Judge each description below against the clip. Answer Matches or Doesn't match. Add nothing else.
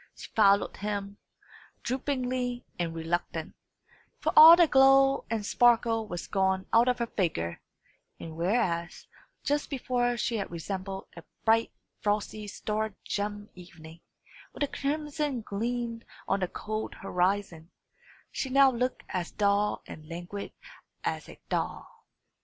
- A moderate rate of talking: Doesn't match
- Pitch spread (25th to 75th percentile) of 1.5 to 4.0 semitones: Doesn't match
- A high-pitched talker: Matches